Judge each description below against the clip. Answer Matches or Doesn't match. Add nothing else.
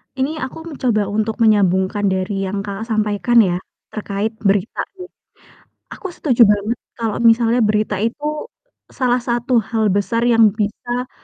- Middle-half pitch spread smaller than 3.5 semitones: Matches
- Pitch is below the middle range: Doesn't match